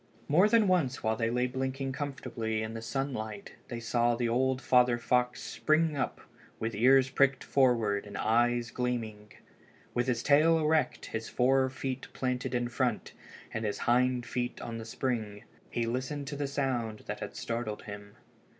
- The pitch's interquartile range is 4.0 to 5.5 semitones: No, average, 2.7 semitones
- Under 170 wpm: No, average, 175 wpm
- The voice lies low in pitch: Yes, low, 125 Hz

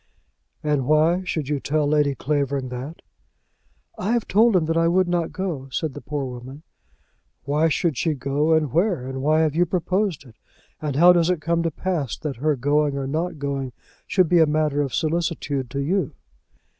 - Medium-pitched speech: Yes, medium, 155 Hz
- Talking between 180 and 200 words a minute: Yes, average, 195 wpm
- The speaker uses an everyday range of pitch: Yes, average, 3.4 semitones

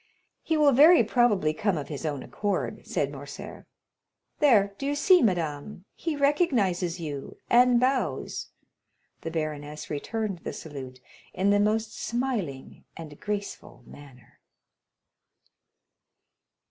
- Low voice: No, high, 195 Hz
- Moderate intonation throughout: No, wide, 8.4 semitones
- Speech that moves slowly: Yes, slow, 120 wpm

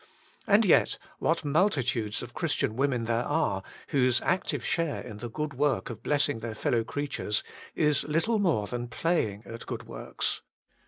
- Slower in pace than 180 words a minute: Yes, average, 160 wpm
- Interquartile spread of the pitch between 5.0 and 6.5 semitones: Yes, average, 5.3 semitones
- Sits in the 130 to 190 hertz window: Yes, low, 135 Hz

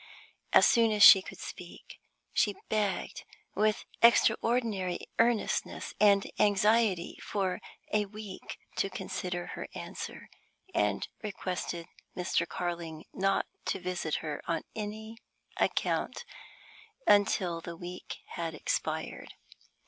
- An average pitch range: Yes, average, 3.3 semitones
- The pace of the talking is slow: Yes, slow, 110 wpm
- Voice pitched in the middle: No, high, 195 Hz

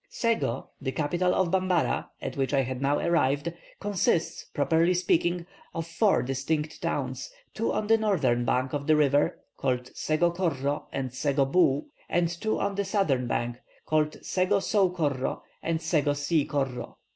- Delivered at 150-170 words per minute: Yes, average, 160 wpm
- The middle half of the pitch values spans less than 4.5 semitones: No, average, 4.9 semitones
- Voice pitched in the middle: Yes, medium, 155 Hz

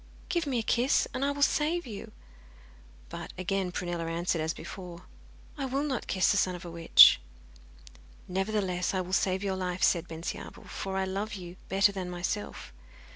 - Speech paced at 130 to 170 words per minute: No, average, 180 wpm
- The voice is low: No, high, 190 Hz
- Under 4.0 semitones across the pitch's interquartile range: Yes, average, 3.4 semitones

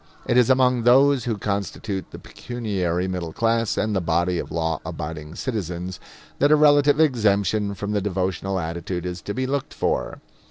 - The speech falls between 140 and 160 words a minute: No, average, 170 wpm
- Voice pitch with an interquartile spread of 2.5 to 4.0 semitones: No, wide, 5.5 semitones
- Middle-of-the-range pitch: No, low, 100 Hz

